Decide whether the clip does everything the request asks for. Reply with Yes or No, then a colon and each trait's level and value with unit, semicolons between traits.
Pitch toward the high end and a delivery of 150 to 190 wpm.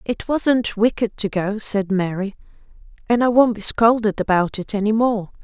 Yes: high, 215 Hz; average, 175 wpm